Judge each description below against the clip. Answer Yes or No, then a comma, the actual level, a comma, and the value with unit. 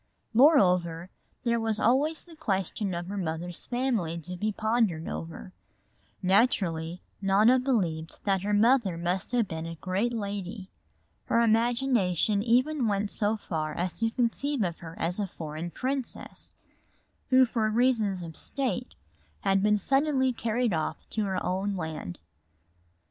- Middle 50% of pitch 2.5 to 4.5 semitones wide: No, average, 5.3 semitones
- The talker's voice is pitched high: Yes, high, 205 Hz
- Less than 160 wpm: Yes, average, 145 wpm